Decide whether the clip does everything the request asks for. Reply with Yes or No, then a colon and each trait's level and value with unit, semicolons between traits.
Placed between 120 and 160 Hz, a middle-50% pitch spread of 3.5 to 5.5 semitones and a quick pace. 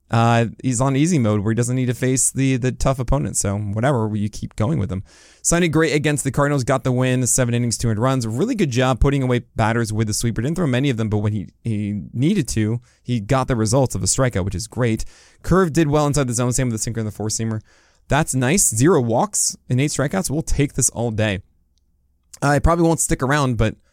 Yes: low, 125 Hz; average, 3.9 semitones; fast, 245 wpm